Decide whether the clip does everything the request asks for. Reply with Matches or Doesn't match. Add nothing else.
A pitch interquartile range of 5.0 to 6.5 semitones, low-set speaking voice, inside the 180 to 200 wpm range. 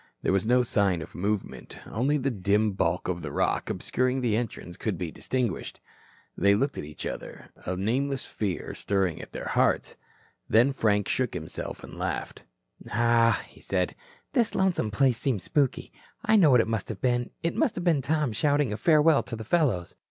Matches